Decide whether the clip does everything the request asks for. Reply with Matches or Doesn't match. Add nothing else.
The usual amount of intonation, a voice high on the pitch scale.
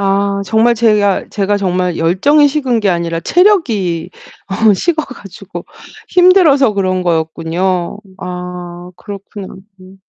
Matches